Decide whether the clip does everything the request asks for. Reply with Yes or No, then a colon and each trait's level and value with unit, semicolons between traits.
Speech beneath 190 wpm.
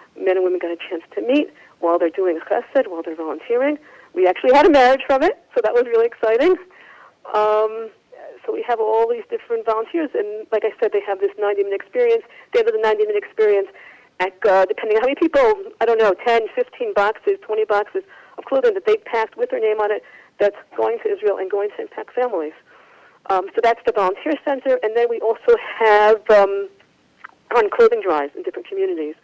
No: fast, 205 wpm